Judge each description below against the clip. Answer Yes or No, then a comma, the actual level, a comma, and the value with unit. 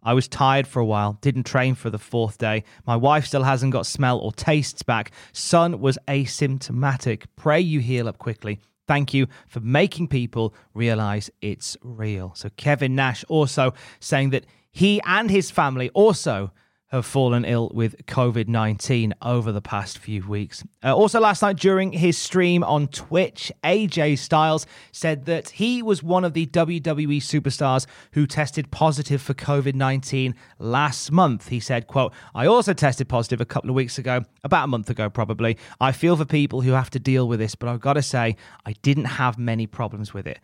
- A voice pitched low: Yes, low, 130 Hz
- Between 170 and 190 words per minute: Yes, average, 185 wpm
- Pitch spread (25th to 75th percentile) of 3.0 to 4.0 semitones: No, average, 4.4 semitones